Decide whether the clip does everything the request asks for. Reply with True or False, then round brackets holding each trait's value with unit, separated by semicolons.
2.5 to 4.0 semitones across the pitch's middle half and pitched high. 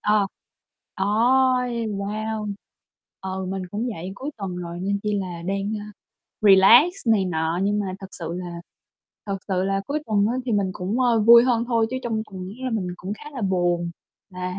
True (3.4 semitones; 200 Hz)